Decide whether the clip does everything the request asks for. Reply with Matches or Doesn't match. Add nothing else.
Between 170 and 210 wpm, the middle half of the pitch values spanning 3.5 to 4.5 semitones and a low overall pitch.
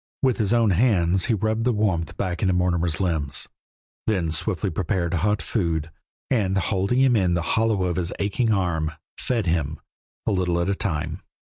Matches